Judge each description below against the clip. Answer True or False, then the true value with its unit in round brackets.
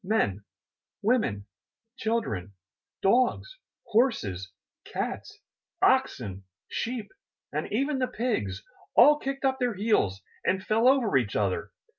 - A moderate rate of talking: False (110 wpm)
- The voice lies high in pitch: True (220 Hz)